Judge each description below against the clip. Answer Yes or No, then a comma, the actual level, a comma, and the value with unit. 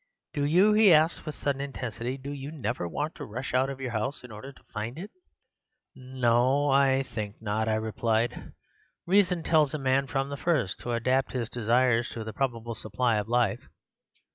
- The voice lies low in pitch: Yes, low, 130 Hz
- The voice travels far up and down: No, average, 3.6 semitones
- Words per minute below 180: No, average, 190 wpm